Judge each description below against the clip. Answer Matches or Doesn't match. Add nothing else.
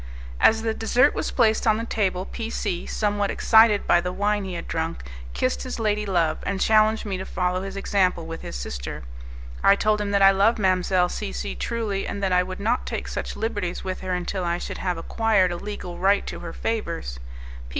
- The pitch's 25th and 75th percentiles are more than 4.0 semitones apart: Doesn't match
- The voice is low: Doesn't match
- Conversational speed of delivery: Doesn't match